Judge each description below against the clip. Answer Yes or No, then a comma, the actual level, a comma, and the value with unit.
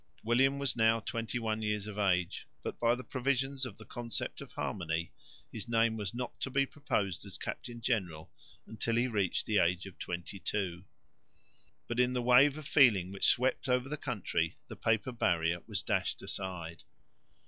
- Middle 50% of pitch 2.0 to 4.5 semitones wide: No, average, 4.9 semitones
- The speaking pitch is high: No, low, 110 Hz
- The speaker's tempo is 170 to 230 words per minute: Yes, average, 180 wpm